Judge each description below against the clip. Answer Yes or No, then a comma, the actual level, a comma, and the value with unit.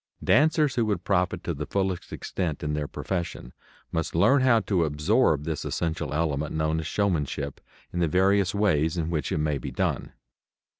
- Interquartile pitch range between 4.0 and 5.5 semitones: Yes, average, 4.6 semitones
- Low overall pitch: Yes, very low, 85 Hz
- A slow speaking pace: No, average, 180 wpm